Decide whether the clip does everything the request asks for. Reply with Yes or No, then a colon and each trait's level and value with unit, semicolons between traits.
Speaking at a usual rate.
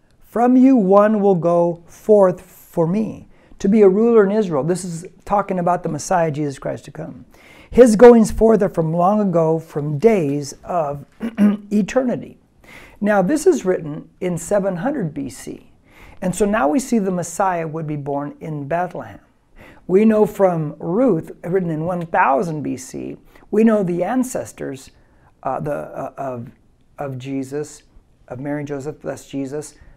Yes: average, 155 wpm